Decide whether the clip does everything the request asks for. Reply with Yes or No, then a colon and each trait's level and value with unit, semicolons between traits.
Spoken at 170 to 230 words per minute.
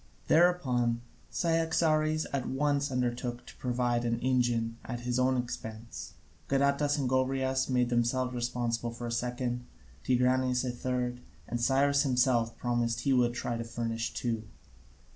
No: average, 145 wpm